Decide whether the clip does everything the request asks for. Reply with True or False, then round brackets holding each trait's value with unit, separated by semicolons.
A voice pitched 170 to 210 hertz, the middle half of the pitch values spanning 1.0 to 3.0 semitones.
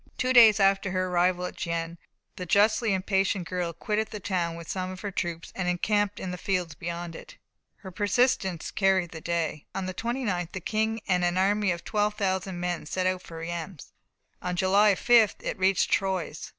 True (185 Hz; 2.7 semitones)